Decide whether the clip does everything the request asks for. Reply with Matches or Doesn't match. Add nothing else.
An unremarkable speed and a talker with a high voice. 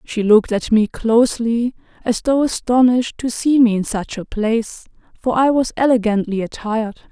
Matches